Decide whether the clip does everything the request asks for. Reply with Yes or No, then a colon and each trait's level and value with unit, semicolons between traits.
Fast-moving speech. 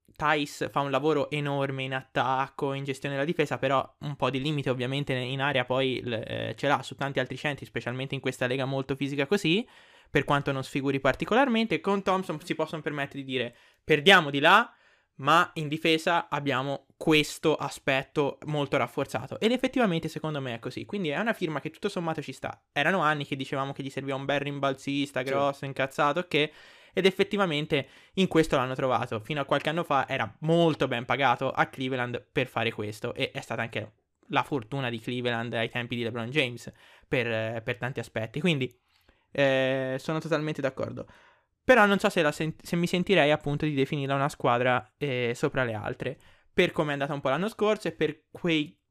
Yes: fast, 190 wpm